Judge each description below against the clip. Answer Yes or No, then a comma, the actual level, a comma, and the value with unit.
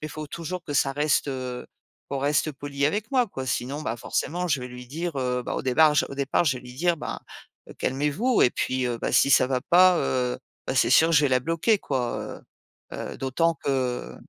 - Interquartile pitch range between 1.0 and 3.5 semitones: No, average, 4.3 semitones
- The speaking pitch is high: No, medium, 140 Hz